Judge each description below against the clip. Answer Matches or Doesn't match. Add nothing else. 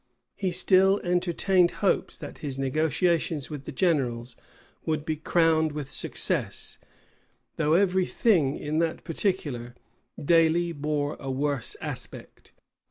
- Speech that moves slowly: Matches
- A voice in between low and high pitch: Matches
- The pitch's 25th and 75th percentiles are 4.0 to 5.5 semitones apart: Doesn't match